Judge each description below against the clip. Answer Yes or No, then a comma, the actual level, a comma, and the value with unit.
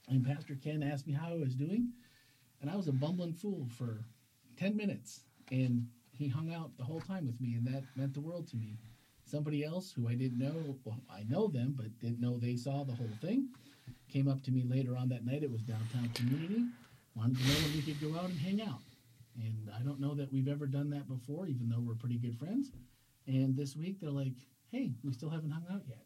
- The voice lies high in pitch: No, low, 135 Hz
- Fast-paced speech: Yes, fast, 235 wpm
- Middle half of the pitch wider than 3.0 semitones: Yes, average, 3.7 semitones